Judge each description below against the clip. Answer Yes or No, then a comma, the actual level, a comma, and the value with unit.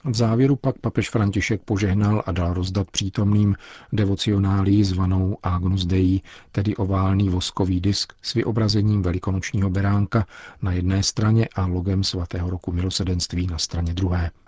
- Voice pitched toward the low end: Yes, very low, 95 Hz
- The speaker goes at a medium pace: Yes, average, 135 wpm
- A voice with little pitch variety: Yes, narrow, 2.3 semitones